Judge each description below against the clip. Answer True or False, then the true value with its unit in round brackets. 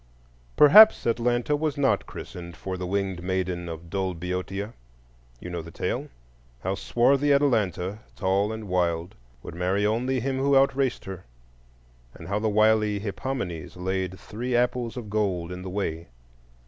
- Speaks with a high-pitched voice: False (100 Hz)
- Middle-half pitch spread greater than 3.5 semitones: True (5.1 semitones)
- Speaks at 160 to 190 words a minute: False (150 wpm)